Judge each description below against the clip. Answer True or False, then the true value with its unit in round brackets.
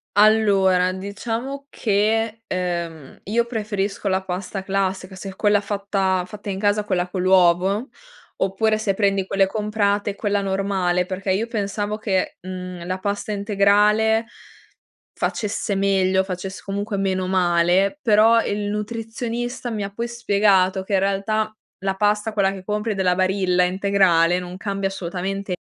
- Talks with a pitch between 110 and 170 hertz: False (195 Hz)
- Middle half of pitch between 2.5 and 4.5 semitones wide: False (2.0 semitones)